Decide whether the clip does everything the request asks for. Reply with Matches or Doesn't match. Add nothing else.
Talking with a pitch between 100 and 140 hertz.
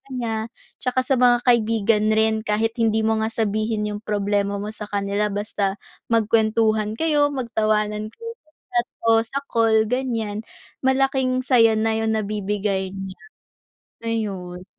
Doesn't match